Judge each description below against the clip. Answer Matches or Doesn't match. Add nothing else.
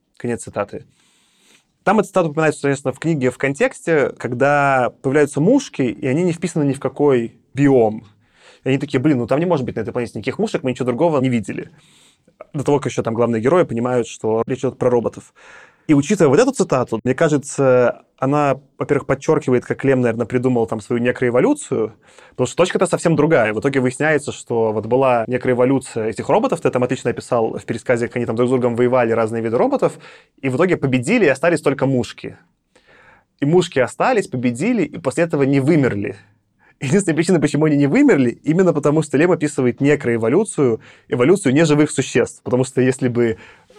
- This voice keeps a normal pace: Doesn't match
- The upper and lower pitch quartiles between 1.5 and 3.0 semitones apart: Doesn't match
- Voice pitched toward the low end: Matches